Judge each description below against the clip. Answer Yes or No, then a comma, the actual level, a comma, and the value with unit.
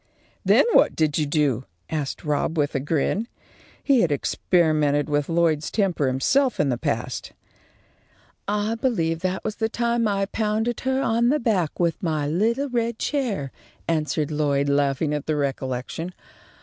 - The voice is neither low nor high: Yes, medium, 165 Hz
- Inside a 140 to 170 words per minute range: Yes, average, 160 wpm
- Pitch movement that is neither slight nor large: No, wide, 7.2 semitones